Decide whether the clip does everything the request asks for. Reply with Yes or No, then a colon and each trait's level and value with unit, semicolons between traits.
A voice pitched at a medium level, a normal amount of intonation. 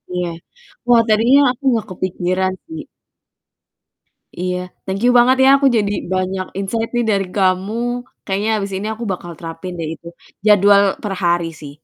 No: high, 195 Hz; average, 3.5 semitones